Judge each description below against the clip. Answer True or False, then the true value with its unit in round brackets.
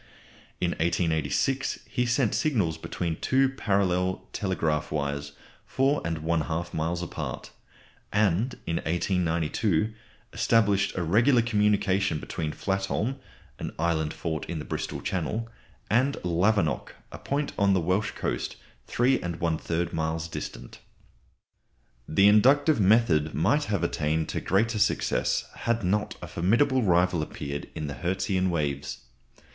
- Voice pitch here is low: True (90 Hz)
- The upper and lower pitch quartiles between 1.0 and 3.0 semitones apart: False (5.2 semitones)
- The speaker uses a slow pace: True (125 wpm)